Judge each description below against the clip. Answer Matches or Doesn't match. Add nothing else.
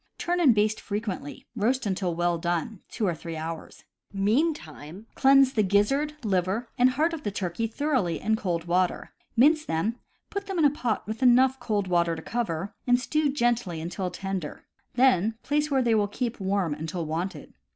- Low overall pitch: Doesn't match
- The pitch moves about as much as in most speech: Doesn't match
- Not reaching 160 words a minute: Doesn't match